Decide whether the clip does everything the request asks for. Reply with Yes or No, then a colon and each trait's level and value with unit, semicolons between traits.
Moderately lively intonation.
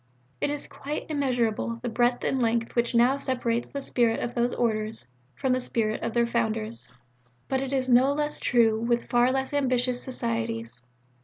No: narrow, 2.2 semitones